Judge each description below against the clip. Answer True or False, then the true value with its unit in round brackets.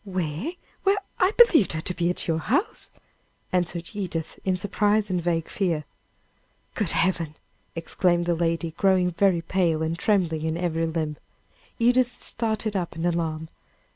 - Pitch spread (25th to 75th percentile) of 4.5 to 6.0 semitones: False (3.6 semitones)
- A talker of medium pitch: True (175 Hz)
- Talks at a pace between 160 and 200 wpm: False (150 wpm)